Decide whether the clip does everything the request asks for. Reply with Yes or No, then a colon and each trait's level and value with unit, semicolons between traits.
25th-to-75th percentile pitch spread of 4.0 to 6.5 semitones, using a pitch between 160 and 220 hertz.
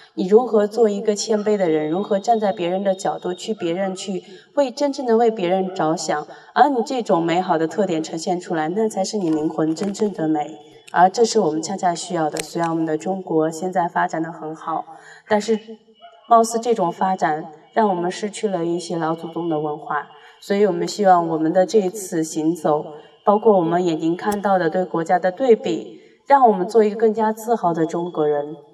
Yes: average, 4.8 semitones; medium, 185 Hz